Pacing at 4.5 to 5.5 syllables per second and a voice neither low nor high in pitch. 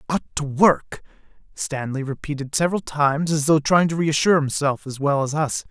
Yes: 5.4 syllables/s; medium, 150 Hz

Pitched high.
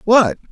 Yes: high, 210 Hz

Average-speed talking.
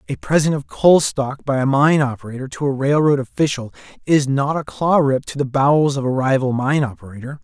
No: fast, 210 wpm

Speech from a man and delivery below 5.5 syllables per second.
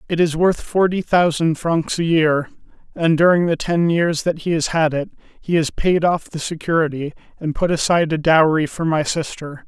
Yes: male; 5.0 syllables/s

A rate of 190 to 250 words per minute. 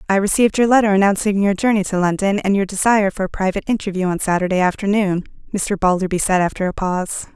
Yes: fast, 205 wpm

